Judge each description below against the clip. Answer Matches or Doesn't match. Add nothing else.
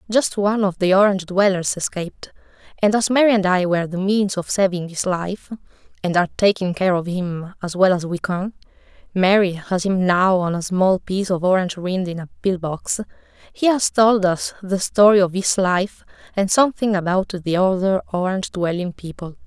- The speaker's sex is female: Matches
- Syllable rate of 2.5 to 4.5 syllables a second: Matches